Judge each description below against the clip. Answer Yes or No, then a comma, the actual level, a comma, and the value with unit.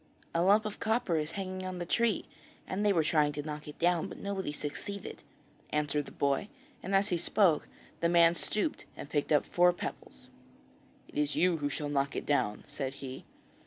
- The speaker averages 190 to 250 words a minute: Yes, average, 200 wpm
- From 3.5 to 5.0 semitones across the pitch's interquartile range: Yes, average, 4.2 semitones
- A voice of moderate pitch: Yes, medium, 165 Hz